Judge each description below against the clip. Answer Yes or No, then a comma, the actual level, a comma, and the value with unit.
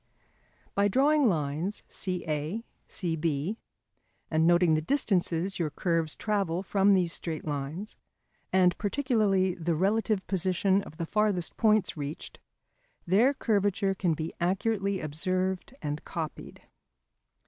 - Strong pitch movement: No, average, 3.8 semitones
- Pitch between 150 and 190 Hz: Yes, medium, 185 Hz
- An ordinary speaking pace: No, slow, 115 wpm